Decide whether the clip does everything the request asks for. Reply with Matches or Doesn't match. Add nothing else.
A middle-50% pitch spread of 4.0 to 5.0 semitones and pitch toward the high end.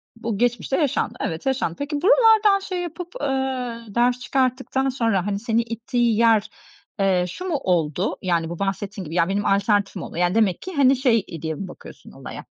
Doesn't match